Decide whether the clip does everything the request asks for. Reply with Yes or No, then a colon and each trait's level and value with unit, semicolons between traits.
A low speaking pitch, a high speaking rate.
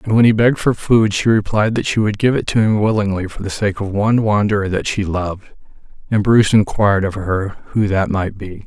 Yes: low, 105 Hz; fast, 235 wpm